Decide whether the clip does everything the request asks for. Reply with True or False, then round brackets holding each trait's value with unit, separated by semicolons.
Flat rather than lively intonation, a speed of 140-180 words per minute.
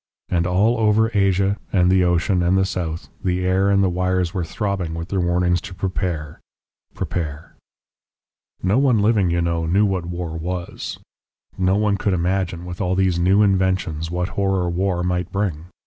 True (1.9 semitones; 175 wpm)